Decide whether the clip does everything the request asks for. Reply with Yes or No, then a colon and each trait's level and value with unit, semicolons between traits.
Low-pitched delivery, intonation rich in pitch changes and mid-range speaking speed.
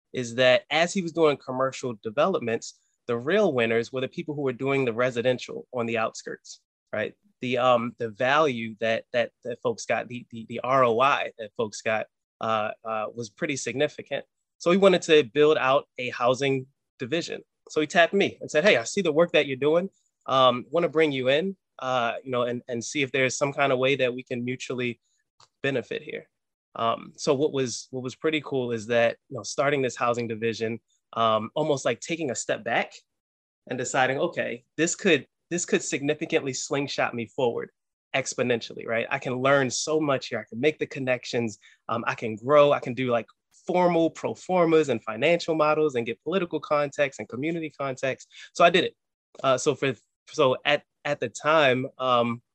No: low, 130 Hz; average, 4.3 semitones; average, 195 wpm